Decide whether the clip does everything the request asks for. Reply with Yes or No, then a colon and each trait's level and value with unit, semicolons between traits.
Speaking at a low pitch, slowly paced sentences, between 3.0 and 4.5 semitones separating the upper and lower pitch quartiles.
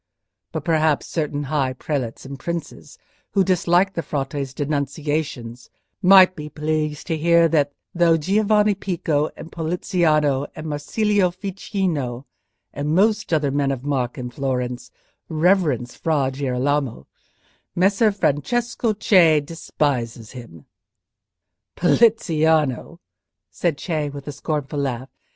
No: medium, 155 Hz; slow, 115 wpm; average, 4.2 semitones